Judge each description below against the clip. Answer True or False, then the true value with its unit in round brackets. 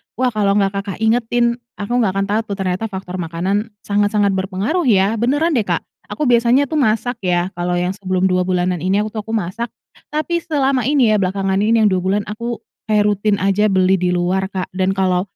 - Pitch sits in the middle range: False (205 Hz)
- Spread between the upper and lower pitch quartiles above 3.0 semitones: True (3.6 semitones)